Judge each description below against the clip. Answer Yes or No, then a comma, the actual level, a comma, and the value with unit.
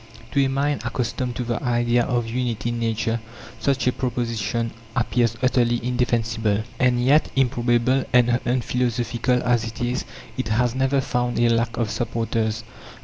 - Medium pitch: No, low, 120 Hz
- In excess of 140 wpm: Yes, average, 150 wpm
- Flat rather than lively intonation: Yes, narrow, 1.4 semitones